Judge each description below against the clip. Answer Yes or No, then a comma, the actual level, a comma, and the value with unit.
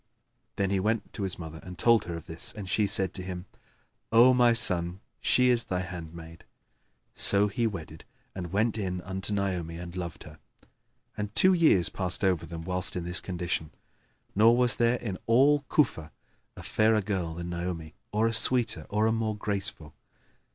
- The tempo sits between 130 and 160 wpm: No, average, 180 wpm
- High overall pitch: No, very low, 95 Hz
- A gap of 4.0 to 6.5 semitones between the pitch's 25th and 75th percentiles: Yes, average, 4.3 semitones